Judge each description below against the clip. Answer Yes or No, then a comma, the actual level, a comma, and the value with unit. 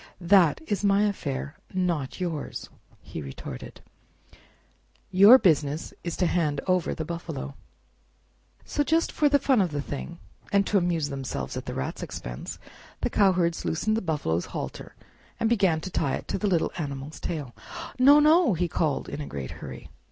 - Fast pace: No, average, 165 wpm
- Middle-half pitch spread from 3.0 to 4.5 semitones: No, wide, 5.6 semitones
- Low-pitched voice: No, medium, 170 Hz